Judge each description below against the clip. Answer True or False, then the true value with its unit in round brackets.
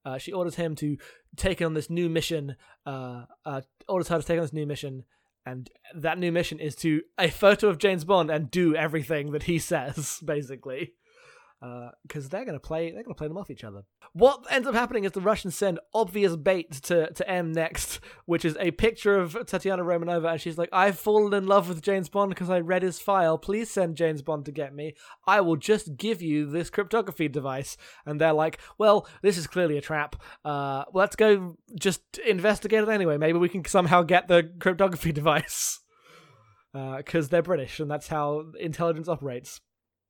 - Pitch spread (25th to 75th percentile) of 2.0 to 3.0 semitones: False (4.2 semitones)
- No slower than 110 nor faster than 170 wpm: False (205 wpm)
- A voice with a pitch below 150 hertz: False (170 Hz)